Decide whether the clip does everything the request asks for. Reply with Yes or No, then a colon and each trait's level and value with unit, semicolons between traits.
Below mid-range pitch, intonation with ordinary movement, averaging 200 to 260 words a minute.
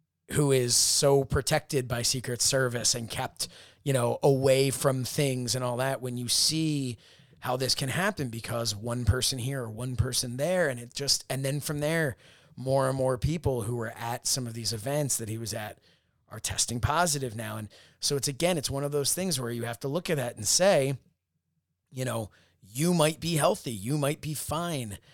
Yes: low, 130 Hz; average, 3.3 semitones; fast, 205 wpm